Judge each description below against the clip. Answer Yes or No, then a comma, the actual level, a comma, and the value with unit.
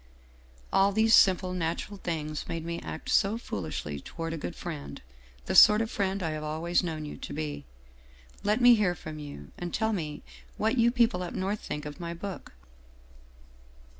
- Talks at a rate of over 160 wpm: Yes, average, 180 wpm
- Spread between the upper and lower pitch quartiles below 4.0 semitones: No, average, 5.0 semitones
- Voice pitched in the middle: Yes, medium, 170 Hz